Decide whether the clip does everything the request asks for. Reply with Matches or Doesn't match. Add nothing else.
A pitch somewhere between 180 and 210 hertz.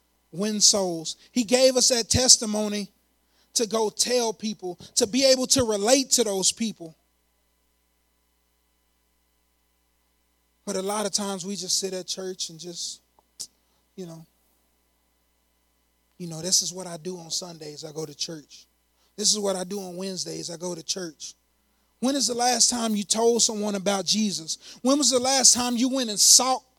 Matches